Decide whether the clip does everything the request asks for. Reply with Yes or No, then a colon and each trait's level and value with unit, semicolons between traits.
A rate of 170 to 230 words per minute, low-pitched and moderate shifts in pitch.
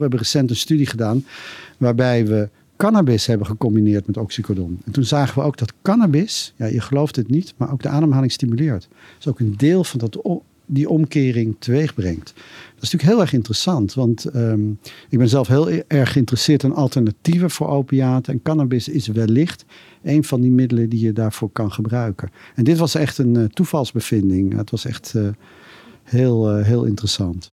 Yes: average, 185 wpm; low, 125 Hz; average, 4.7 semitones